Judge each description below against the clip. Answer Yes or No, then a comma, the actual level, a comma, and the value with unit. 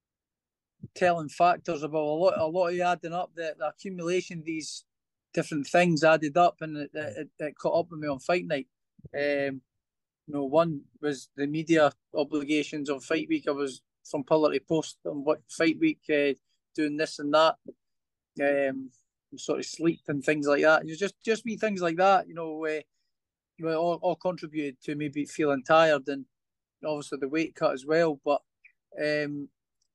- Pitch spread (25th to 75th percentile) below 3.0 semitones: Yes, narrow, 2.6 semitones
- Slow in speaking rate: No, average, 180 wpm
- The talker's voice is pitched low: No, medium, 155 Hz